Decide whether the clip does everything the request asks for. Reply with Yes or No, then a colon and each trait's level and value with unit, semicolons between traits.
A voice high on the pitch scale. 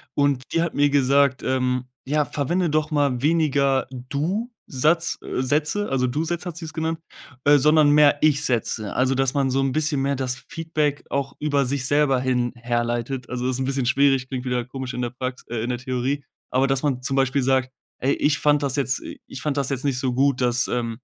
No: low, 135 Hz